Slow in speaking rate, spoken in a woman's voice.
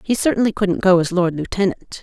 No: fast, 205 wpm; female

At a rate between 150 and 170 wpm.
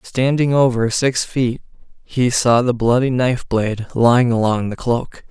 Yes: average, 160 wpm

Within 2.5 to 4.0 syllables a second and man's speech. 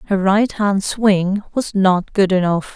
No: 3.7 syllables/s; female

